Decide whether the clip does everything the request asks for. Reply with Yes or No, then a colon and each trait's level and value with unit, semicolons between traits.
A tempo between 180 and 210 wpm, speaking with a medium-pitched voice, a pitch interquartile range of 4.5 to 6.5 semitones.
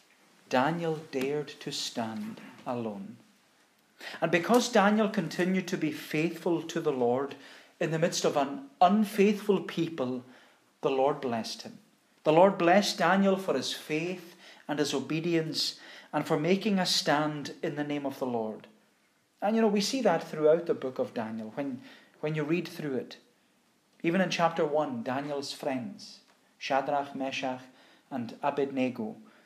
No: average, 150 wpm; medium, 160 Hz; average, 4.9 semitones